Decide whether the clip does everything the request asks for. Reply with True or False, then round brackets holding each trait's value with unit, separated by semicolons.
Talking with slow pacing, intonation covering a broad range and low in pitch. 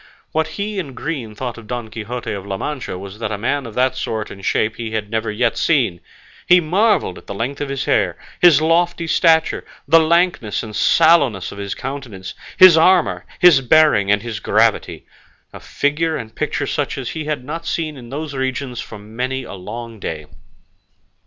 False (190 wpm; 6.5 semitones; 130 Hz)